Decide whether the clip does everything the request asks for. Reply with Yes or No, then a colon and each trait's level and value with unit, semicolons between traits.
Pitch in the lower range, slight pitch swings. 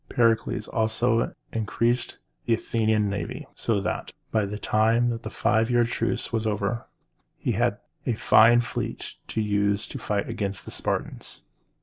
Yes: low, 110 Hz; narrow, 1.9 semitones